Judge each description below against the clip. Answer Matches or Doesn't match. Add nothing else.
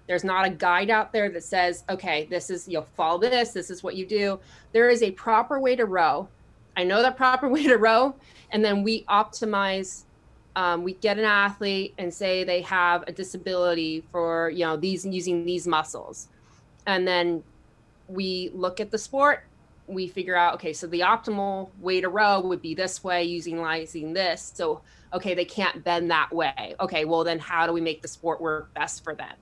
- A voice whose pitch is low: Doesn't match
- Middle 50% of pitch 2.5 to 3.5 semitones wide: Matches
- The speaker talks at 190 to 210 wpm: Matches